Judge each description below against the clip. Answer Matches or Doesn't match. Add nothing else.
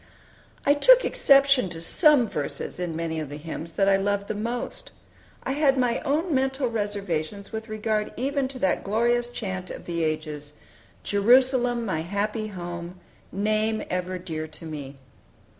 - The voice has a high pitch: Matches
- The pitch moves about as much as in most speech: Doesn't match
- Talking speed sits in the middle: Matches